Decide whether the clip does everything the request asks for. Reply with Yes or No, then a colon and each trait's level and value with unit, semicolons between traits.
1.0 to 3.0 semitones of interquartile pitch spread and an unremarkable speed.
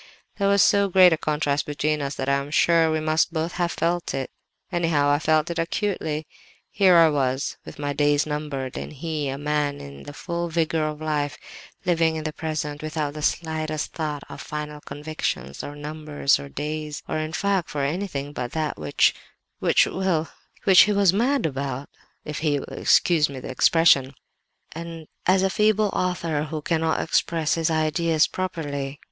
Yes: narrow, 2.5 semitones; average, 175 wpm